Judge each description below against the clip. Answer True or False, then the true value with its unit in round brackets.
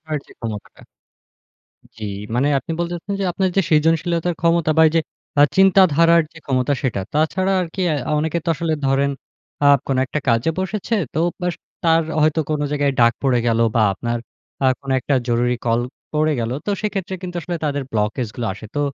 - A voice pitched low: False (155 Hz)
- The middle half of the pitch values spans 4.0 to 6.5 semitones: True (5.4 semitones)